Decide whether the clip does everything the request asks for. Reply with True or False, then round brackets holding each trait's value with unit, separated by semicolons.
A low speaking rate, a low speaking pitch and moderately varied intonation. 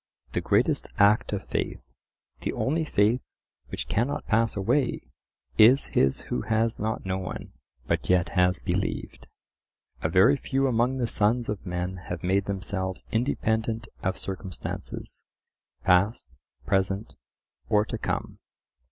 True (130 wpm; 105 Hz; 3.6 semitones)